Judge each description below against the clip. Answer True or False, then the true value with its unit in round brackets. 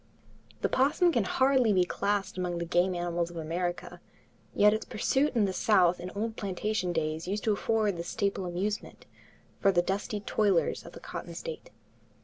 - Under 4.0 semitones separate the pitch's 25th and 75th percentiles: True (3.6 semitones)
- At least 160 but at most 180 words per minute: True (175 wpm)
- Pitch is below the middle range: False (195 Hz)